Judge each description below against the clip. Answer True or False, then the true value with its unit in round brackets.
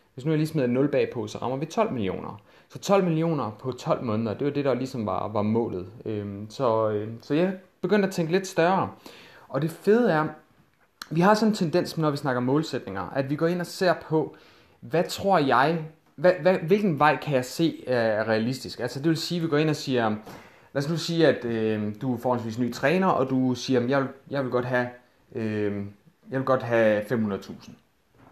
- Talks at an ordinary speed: True (210 wpm)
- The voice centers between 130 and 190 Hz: True (135 Hz)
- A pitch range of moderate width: False (6.0 semitones)